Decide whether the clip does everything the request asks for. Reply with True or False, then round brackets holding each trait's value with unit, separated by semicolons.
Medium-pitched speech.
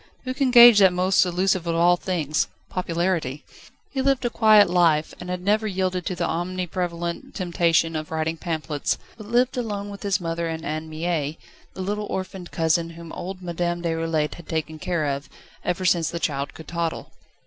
True (175 Hz)